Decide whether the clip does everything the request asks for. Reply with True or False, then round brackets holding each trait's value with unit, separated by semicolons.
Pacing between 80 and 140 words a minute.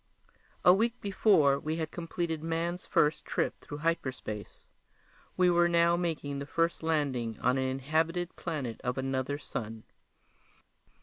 True (135 wpm)